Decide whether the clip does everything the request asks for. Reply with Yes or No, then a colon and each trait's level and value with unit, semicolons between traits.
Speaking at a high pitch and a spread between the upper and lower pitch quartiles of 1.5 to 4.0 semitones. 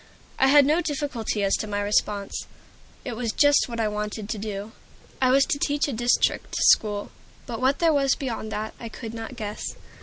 No: high, 230 Hz; average, 4.5 semitones